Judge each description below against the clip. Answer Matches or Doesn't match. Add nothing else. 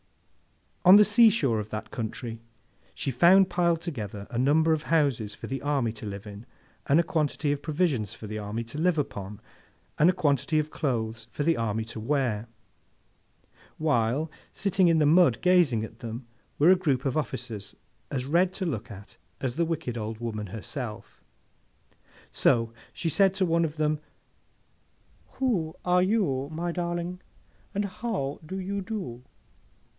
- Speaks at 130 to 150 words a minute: Doesn't match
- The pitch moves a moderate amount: Doesn't match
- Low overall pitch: Doesn't match